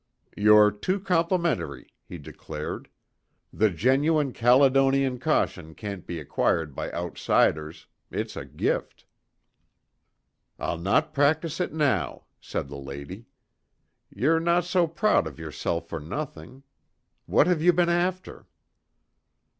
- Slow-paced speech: Yes, slow, 115 wpm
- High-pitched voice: No, low, 130 Hz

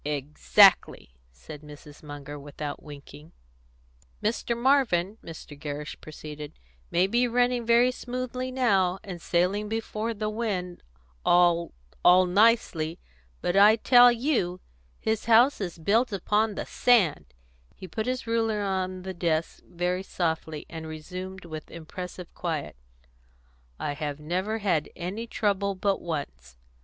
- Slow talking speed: Yes, slow, 130 wpm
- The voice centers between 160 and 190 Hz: Yes, medium, 185 Hz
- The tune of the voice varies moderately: No, wide, 5.9 semitones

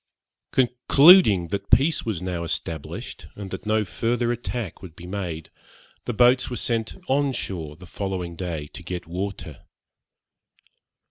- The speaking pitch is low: Yes, low, 100 Hz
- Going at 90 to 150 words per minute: Yes, average, 140 wpm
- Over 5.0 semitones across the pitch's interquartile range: Yes, wide, 5.6 semitones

